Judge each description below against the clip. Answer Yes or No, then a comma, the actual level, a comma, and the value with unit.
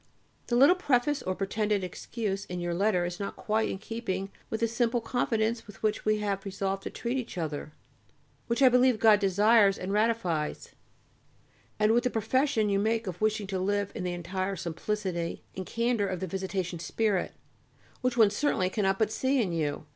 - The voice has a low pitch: No, high, 205 Hz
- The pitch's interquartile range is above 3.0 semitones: Yes, average, 3.5 semitones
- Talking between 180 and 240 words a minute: Yes, average, 185 wpm